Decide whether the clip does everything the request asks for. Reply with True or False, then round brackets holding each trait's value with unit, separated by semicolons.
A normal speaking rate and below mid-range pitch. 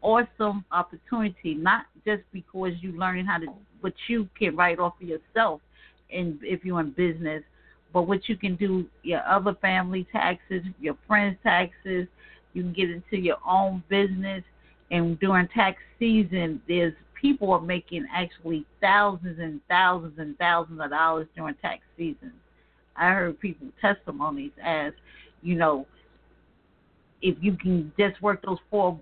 False (155 wpm; 185 Hz)